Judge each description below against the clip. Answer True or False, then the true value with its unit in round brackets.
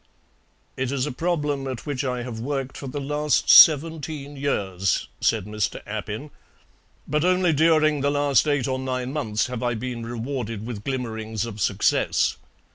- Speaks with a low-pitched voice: True (130 Hz)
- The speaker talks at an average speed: True (160 wpm)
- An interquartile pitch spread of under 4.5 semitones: True (4.1 semitones)